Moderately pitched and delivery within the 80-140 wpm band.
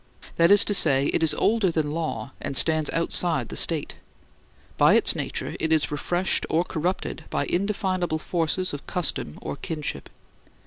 No: medium, 165 Hz; average, 165 wpm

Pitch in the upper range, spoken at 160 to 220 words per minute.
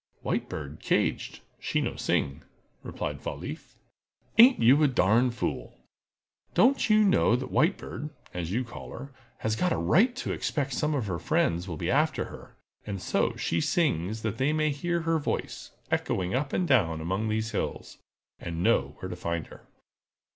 No: low, 115 Hz; average, 175 wpm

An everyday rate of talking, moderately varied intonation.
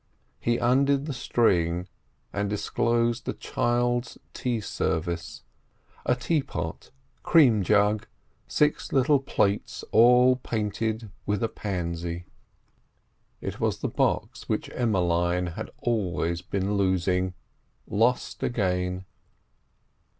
No: slow, 95 wpm; average, 5.0 semitones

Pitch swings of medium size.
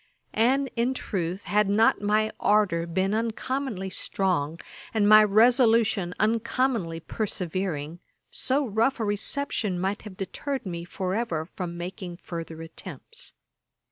Yes: average, 4.4 semitones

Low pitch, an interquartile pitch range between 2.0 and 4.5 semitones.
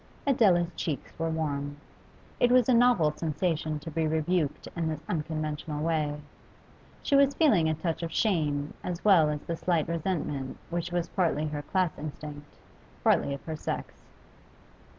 No: medium, 160 Hz; average, 2.8 semitones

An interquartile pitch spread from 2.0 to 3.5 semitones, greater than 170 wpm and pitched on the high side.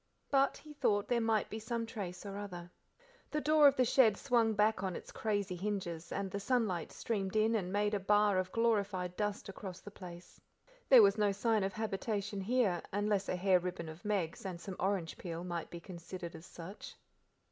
Yes: average, 3.2 semitones; average, 200 wpm; high, 200 Hz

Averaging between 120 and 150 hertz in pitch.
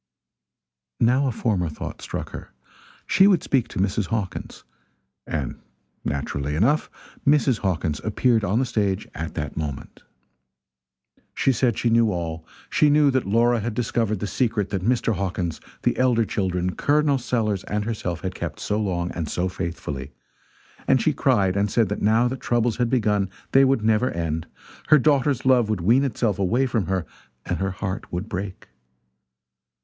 No: low, 105 Hz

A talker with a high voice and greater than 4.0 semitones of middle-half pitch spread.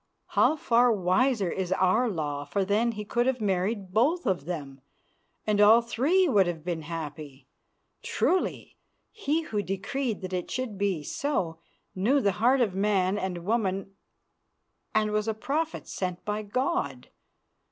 Yes: high, 205 Hz; average, 4.8 semitones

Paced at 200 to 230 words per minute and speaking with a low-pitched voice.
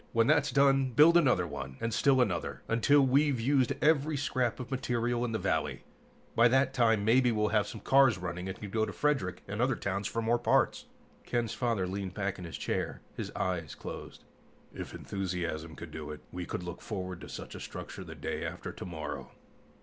Yes: fast, 205 wpm; low, 115 Hz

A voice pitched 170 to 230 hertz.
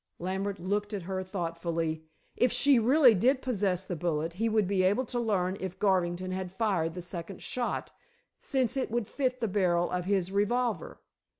Yes: high, 190 Hz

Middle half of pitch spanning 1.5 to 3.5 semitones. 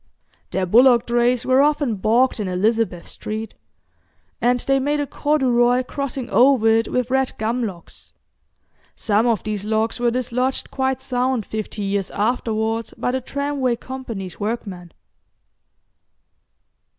Yes: average, 3.1 semitones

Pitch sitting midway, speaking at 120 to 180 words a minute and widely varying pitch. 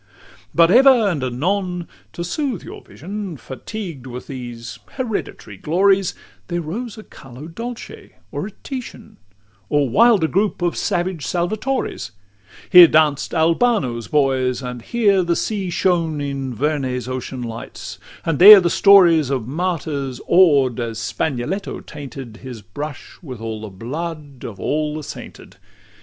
Yes: medium, 155 Hz; average, 140 wpm; wide, 6.6 semitones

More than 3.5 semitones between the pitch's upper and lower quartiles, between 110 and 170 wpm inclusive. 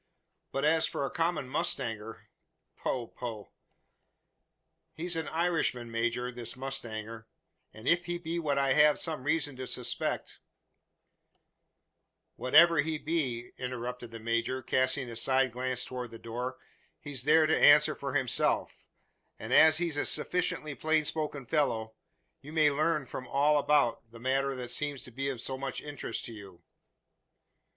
Yes: average, 4.0 semitones; average, 155 wpm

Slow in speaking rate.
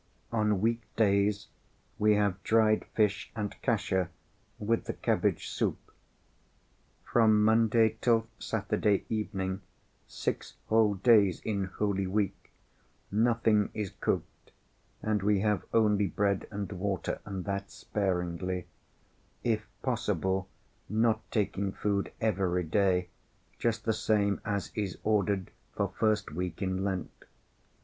Yes: slow, 115 wpm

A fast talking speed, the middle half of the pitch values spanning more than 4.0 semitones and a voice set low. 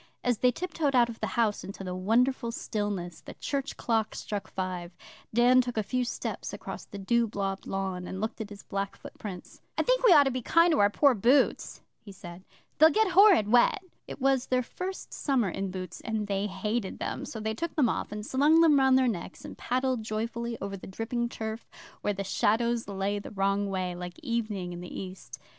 No: fast, 210 wpm; average, 4.5 semitones; high, 220 Hz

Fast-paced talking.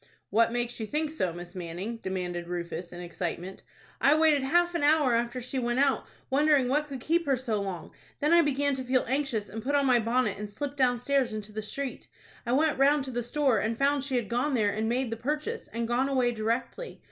Yes: fast, 225 wpm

